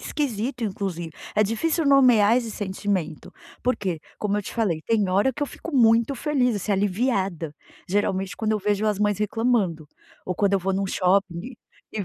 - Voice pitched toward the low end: No, high, 205 Hz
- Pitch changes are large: No, average, 3.6 semitones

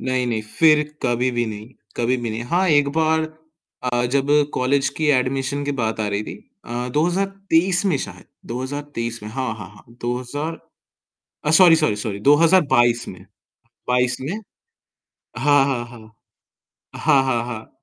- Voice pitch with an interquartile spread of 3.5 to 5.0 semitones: Yes, average, 4.2 semitones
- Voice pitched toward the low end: Yes, low, 130 Hz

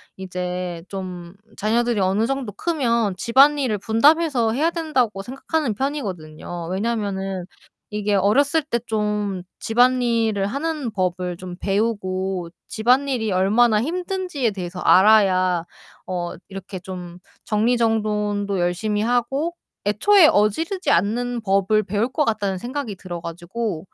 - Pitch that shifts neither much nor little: Yes, average, 4.6 semitones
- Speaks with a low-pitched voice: No, high, 210 Hz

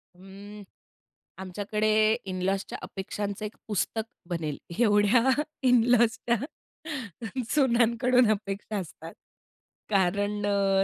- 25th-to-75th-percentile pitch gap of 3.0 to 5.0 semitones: No, narrow, 2.6 semitones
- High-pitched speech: Yes, high, 205 Hz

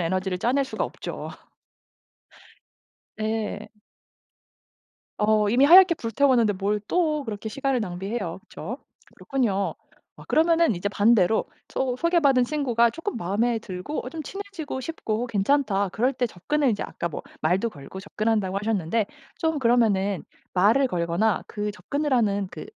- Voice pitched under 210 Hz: No, high, 225 Hz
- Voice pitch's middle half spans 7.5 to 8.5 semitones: No, average, 5.3 semitones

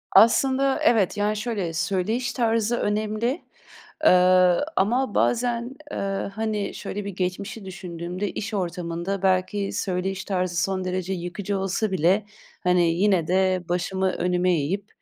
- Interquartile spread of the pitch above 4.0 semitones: No, average, 2.9 semitones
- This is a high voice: Yes, high, 195 Hz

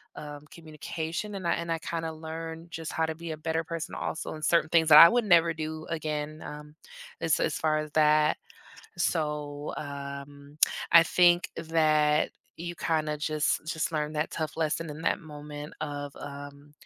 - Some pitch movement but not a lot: No, narrow, 1.6 semitones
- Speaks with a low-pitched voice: No, medium, 155 Hz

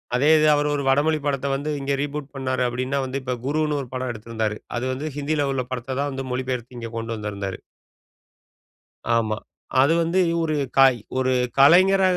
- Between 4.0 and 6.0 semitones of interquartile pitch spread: No, average, 2.9 semitones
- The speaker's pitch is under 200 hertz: Yes, low, 135 Hz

